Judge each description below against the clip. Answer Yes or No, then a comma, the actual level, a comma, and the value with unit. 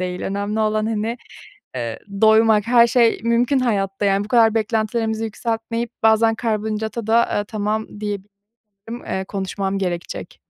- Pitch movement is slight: Yes, narrow, 2.0 semitones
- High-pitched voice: Yes, high, 220 Hz